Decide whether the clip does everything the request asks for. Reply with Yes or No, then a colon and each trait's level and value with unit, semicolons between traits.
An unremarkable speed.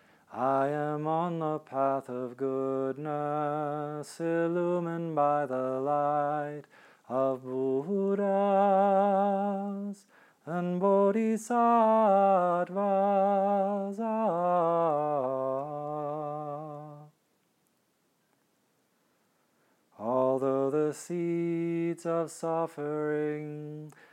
No: slow, 50 wpm